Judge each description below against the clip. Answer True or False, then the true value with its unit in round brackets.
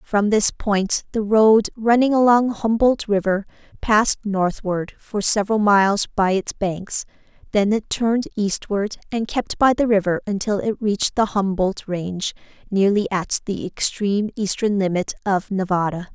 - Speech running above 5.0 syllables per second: False (4.5 syllables/s)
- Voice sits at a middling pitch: False (205 Hz)